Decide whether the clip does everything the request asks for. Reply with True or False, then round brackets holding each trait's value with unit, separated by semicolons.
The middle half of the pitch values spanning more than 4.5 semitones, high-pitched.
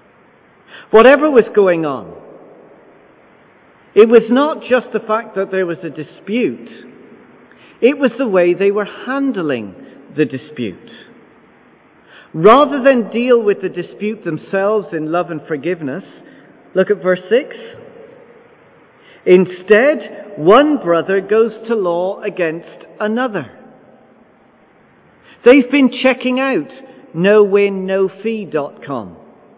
True (5.6 semitones; 210 Hz)